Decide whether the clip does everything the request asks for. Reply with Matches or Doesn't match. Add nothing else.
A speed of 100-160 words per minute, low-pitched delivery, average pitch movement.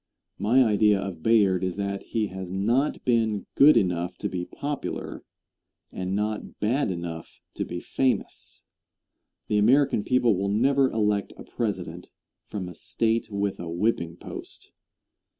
Matches